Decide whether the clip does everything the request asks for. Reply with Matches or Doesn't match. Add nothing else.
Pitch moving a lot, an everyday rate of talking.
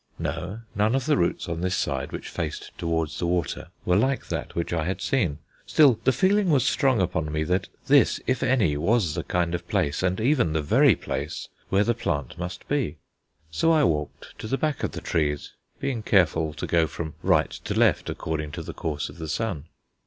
Doesn't match